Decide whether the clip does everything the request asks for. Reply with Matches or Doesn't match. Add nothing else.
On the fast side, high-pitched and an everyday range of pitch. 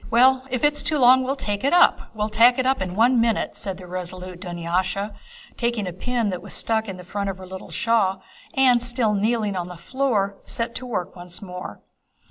Matches